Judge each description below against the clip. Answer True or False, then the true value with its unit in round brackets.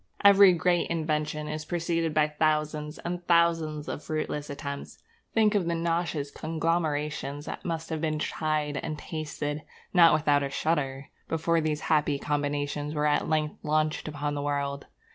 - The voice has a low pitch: False (155 Hz)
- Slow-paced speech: False (155 wpm)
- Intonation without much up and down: True (2.0 semitones)